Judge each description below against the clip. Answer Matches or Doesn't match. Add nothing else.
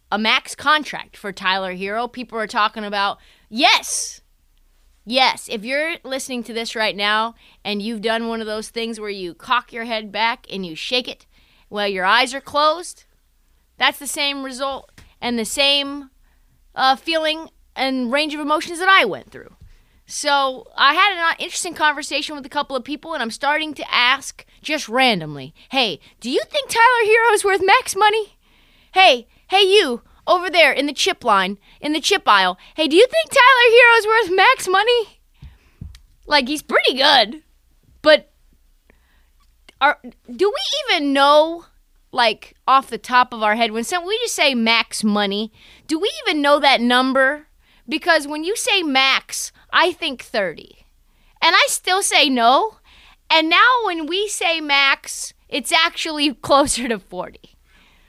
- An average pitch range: Doesn't match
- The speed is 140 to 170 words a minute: Matches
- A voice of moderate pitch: Doesn't match